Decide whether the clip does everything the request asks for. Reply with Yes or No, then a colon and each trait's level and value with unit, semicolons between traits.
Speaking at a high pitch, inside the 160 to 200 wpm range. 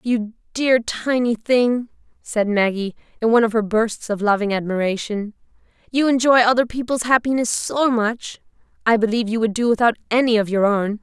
Yes: high, 225 Hz; average, 170 wpm